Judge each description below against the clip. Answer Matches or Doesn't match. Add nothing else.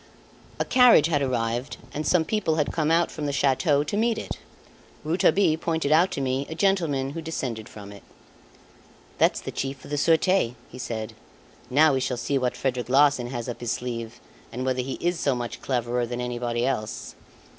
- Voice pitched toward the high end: Doesn't match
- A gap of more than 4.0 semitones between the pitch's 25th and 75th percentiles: Matches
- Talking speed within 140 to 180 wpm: Doesn't match